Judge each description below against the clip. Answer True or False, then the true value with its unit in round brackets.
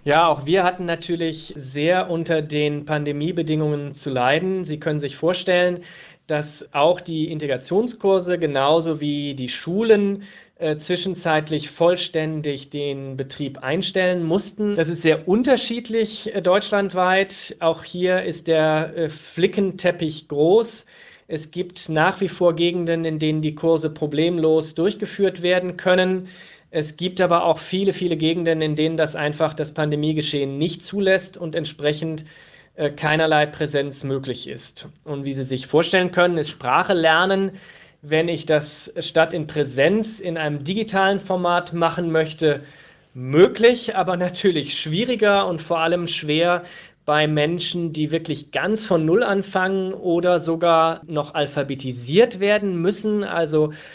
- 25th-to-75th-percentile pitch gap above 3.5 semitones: False (3.2 semitones)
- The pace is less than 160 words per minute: True (135 wpm)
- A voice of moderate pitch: True (165 Hz)